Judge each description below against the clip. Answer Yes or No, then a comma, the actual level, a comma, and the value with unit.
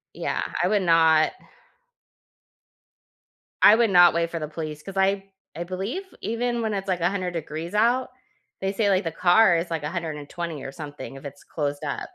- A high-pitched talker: No, medium, 175 Hz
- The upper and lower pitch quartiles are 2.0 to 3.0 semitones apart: No, average, 3.8 semitones